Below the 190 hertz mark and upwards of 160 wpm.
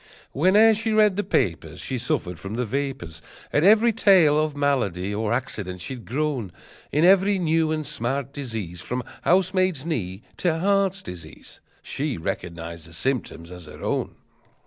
No: low, 135 Hz; average, 155 wpm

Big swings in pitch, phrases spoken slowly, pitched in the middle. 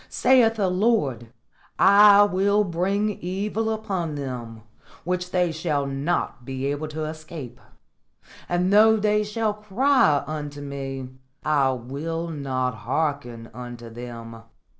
Yes: wide, 7.1 semitones; slow, 120 wpm; medium, 155 Hz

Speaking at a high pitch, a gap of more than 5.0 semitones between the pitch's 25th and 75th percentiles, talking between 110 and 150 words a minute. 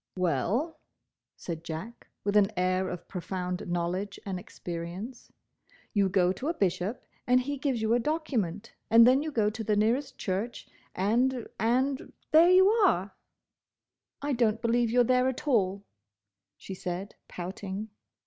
Yes: high, 215 Hz; wide, 5.4 semitones; average, 140 wpm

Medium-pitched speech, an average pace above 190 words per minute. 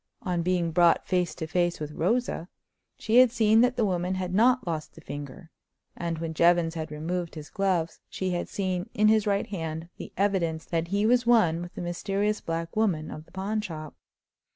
Yes: medium, 180 Hz; average, 200 wpm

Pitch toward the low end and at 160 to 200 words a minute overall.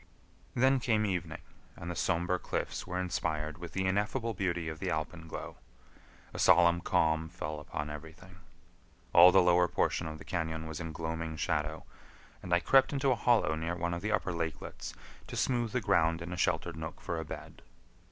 Yes: very low, 85 Hz; average, 185 wpm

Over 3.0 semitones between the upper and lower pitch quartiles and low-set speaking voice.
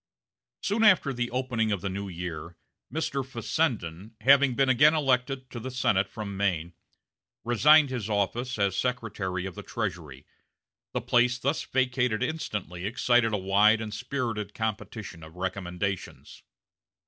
Yes: average, 5.1 semitones; low, 110 Hz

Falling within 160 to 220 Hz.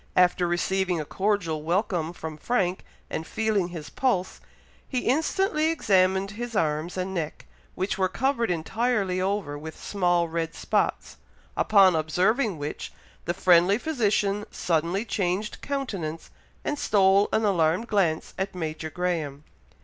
Yes: medium, 185 Hz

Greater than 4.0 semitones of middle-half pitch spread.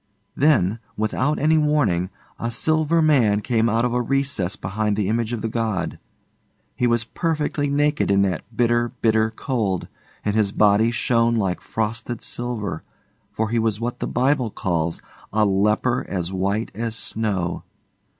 No: average, 3.2 semitones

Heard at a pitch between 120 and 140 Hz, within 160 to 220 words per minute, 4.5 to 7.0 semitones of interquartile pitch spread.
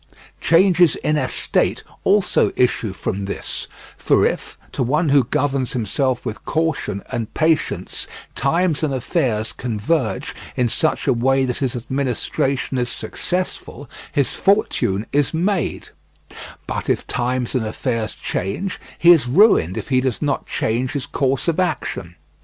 No: low, 135 Hz; average, 140 wpm; average, 4.8 semitones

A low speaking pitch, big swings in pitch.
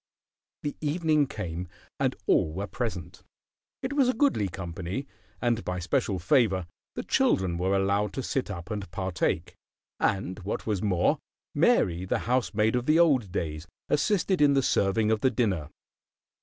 Yes: low, 100 Hz; wide, 6.3 semitones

